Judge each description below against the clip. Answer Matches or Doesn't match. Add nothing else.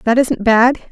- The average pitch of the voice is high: Matches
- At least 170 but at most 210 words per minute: Matches